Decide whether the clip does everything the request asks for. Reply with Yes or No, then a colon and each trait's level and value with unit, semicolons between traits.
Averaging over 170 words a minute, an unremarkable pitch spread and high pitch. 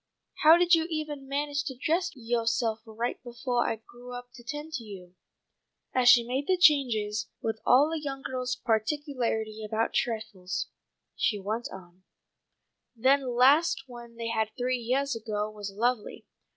No: average, 155 wpm; average, 4.0 semitones; high, 245 Hz